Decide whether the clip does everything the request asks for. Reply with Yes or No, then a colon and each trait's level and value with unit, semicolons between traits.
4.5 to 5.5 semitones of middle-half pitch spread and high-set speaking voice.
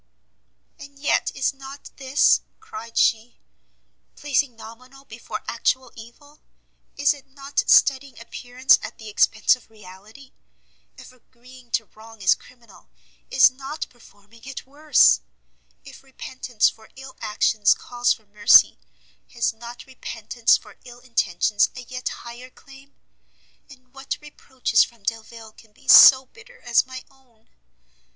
No: average, 3.1 semitones; very high, 250 Hz